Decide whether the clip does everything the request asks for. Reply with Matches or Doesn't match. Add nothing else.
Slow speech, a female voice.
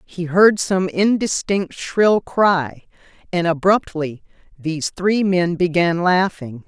Matches